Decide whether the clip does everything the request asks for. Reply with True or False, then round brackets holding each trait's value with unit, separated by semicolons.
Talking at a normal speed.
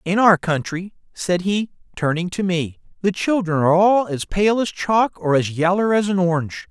True (195 wpm)